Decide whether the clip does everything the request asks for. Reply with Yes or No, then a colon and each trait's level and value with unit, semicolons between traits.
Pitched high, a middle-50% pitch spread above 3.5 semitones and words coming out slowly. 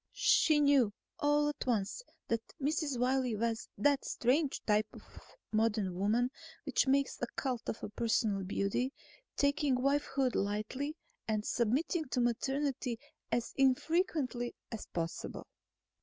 Yes: very high, 250 Hz; average, 4.2 semitones; slow, 125 wpm